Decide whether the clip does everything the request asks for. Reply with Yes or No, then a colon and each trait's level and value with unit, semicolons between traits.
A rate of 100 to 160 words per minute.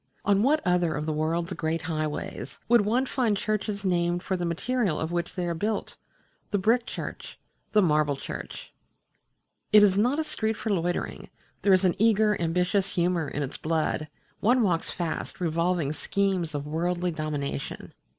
No: average, 170 wpm